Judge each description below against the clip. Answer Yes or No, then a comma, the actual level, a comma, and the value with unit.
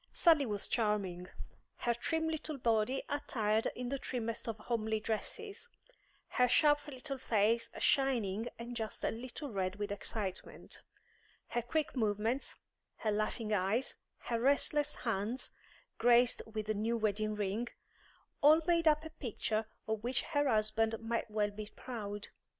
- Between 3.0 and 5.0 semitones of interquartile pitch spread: Yes, average, 4.0 semitones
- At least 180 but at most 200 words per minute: No, average, 145 wpm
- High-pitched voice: Yes, high, 230 Hz